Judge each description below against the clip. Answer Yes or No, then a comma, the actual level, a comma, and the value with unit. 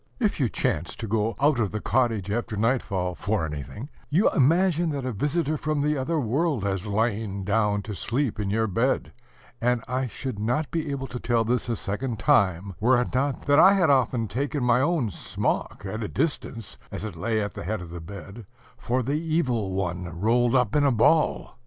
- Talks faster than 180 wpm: Yes, fast, 205 wpm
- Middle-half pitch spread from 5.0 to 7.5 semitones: Yes, average, 5.3 semitones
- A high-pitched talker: No, low, 120 Hz